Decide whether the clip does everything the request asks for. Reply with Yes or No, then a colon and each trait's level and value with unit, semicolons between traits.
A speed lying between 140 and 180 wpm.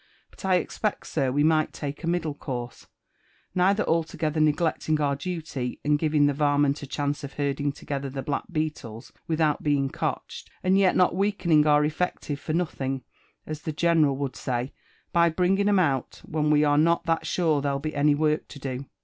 No: average, 190 wpm